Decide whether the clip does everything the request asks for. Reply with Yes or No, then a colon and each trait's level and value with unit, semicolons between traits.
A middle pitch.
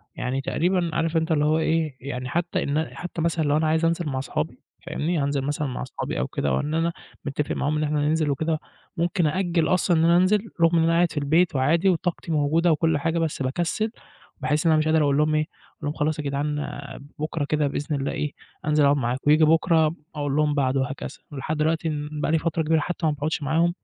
Yes: medium, 155 Hz